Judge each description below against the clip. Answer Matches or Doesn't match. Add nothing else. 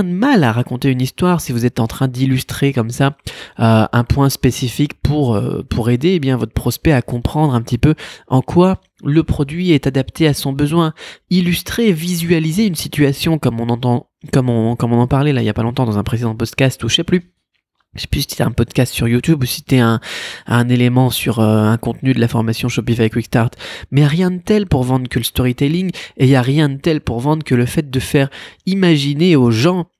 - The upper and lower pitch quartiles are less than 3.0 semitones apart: Doesn't match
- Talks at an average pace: Doesn't match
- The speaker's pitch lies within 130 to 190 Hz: Matches